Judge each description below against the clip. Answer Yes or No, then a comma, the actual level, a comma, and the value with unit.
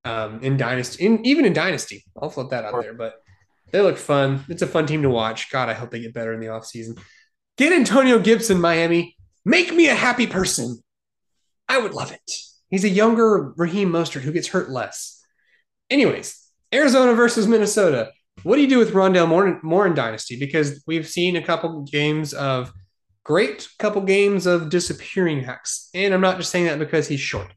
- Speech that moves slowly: No, average, 195 wpm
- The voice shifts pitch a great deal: Yes, wide, 7.7 semitones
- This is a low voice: No, medium, 165 Hz